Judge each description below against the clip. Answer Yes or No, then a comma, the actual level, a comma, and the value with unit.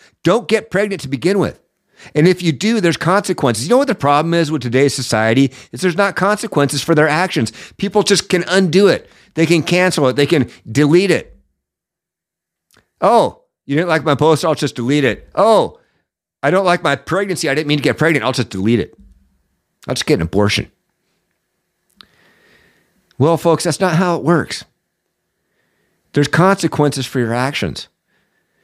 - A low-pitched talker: No, medium, 160 Hz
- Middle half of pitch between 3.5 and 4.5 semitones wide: No, average, 5.2 semitones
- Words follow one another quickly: No, average, 175 wpm